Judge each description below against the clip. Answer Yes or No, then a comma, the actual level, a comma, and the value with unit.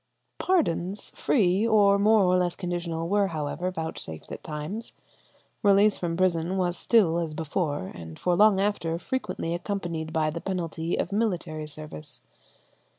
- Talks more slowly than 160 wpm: Yes, average, 145 wpm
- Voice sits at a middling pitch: Yes, medium, 175 Hz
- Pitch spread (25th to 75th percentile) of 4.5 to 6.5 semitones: No, average, 3.7 semitones